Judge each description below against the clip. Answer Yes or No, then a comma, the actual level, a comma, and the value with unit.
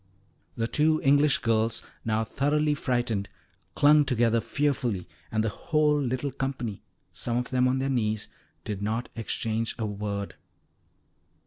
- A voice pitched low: Yes, low, 120 Hz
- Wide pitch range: No, average, 4.2 semitones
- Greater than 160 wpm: No, slow, 135 wpm